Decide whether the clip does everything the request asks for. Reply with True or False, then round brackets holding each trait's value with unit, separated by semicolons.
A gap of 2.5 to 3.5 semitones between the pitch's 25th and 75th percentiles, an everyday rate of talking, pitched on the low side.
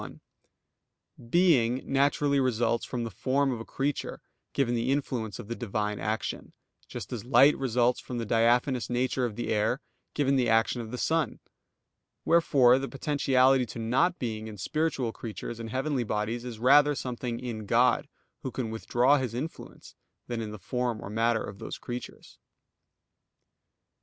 True (2.9 semitones; 160 wpm; 120 Hz)